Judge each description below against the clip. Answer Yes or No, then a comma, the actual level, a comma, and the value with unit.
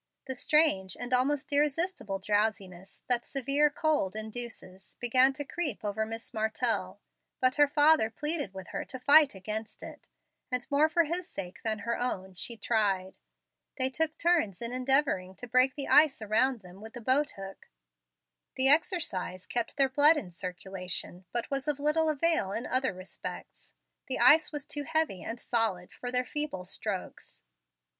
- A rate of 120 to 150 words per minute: No, average, 165 wpm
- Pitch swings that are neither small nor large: No, wide, 6.4 semitones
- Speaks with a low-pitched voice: No, very high, 250 Hz